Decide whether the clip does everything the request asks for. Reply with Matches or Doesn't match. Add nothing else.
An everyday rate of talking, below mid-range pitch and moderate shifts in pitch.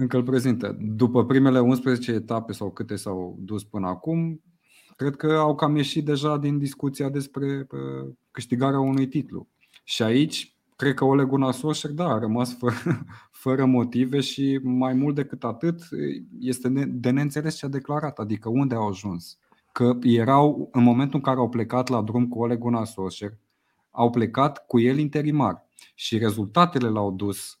Matches